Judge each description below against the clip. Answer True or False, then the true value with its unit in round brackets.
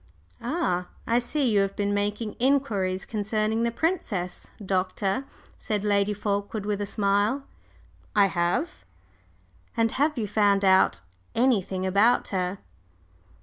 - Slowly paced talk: True (125 wpm)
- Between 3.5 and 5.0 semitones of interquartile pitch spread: False (2.9 semitones)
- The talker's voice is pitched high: True (205 Hz)